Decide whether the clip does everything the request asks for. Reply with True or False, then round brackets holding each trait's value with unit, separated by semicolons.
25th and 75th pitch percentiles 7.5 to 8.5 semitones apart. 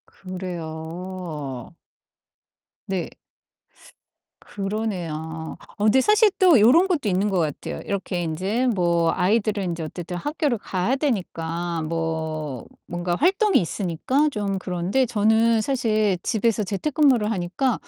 False (5.2 semitones)